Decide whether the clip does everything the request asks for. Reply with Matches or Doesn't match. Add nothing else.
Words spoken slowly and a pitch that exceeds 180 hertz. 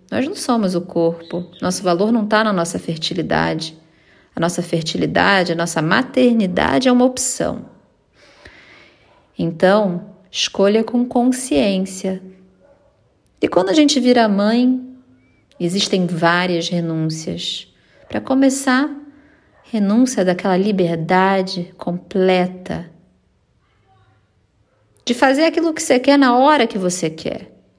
Matches